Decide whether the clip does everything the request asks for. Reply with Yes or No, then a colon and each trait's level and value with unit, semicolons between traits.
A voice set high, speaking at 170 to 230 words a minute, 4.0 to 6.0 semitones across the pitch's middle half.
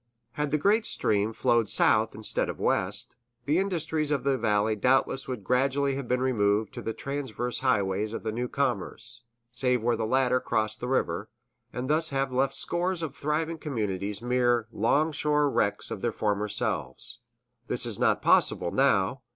No: low, 125 Hz; average, 175 wpm; average, 4.5 semitones